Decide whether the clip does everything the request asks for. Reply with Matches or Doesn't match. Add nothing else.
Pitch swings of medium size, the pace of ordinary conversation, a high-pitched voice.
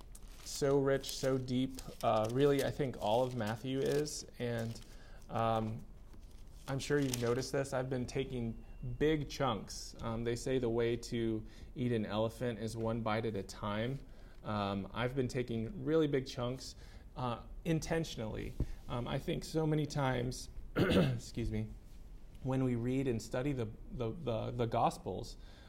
Doesn't match